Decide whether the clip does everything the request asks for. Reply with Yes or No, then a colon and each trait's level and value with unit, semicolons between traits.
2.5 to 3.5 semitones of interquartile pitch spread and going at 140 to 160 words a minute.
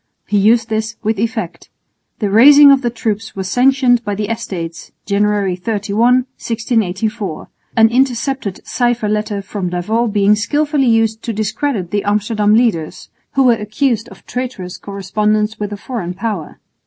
Yes: average, 2.9 semitones; average, 150 wpm